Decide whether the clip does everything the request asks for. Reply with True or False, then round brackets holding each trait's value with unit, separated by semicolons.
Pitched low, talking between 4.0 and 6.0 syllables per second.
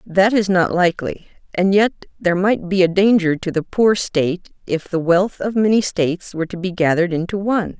False (185 Hz; 5.5 syllables/s)